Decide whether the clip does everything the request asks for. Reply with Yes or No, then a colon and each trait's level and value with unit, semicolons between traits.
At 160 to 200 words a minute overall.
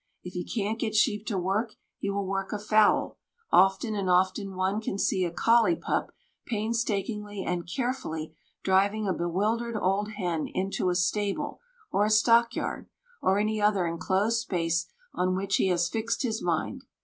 Yes: average, 170 wpm